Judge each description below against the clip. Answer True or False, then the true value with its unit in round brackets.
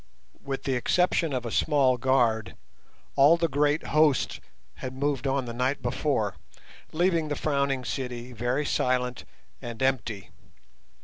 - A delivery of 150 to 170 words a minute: False (135 wpm)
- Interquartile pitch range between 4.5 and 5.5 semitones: False (3.0 semitones)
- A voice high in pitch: False (135 Hz)